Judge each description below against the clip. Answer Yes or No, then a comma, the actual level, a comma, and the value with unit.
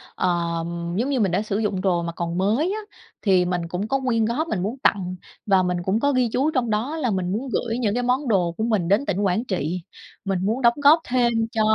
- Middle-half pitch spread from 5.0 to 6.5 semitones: Yes, wide, 5.5 semitones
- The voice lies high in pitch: Yes, high, 210 Hz